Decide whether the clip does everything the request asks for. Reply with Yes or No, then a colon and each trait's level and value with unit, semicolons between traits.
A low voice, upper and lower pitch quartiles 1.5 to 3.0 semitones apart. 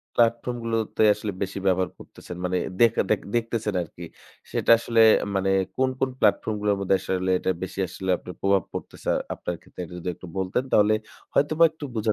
No: low, 105 Hz; average, 3.6 semitones